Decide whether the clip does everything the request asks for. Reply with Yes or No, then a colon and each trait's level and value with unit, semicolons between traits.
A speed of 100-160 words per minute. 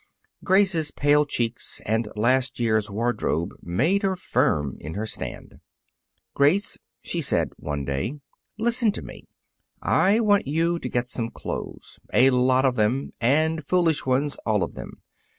Yes: average, 150 wpm